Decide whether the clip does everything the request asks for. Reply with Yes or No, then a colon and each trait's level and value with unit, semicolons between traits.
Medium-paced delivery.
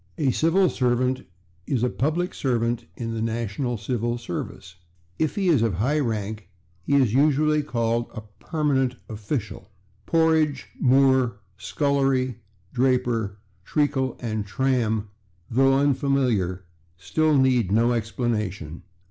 No: slow, 120 wpm